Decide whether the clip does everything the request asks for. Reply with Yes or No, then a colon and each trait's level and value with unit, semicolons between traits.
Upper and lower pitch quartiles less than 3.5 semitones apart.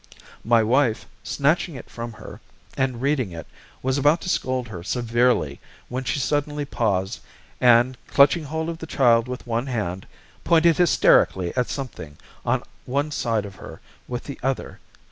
No: average, 3.8 semitones